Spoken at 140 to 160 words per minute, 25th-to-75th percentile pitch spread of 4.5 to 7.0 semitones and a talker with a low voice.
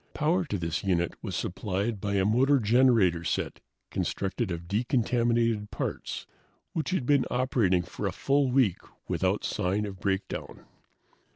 Yes: average, 145 wpm; average, 4.9 semitones; low, 110 Hz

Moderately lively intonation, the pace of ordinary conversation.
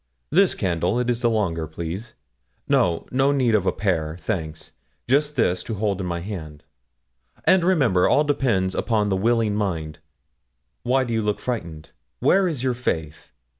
No: wide, 6.3 semitones; average, 170 wpm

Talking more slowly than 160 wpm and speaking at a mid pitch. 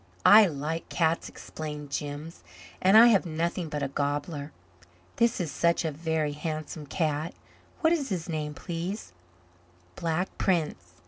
Yes: average, 140 wpm; medium, 160 Hz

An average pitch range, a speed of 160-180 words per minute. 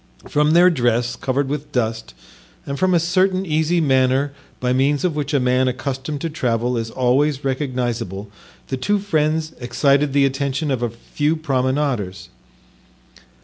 No: average, 3.4 semitones; average, 150 wpm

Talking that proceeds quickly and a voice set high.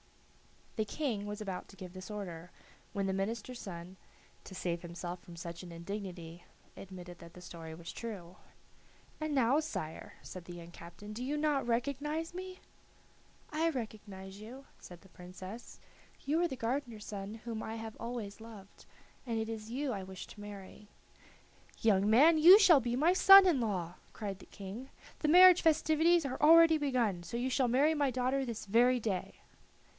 No: average, 175 wpm; high, 220 Hz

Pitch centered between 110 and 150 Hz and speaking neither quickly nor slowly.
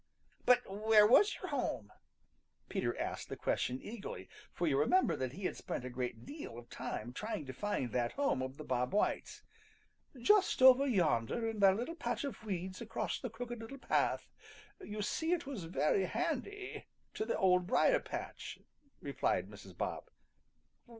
No: high, 210 Hz; average, 165 wpm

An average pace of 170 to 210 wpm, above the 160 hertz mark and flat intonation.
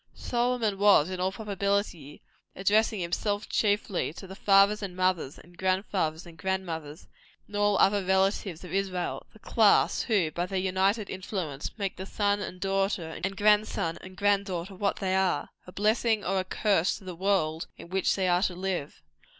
Yes: average, 185 wpm; high, 190 Hz; narrow, 2.1 semitones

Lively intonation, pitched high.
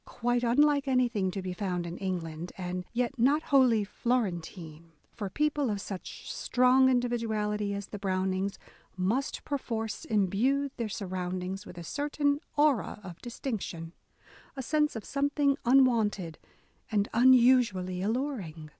Yes: wide, 5.7 semitones; high, 220 Hz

